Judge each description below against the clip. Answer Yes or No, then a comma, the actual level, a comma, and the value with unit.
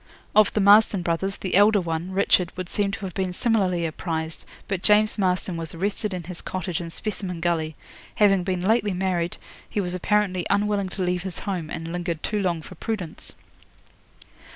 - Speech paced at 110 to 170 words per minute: No, average, 180 wpm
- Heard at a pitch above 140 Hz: Yes, medium, 185 Hz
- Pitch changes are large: No, average, 2.7 semitones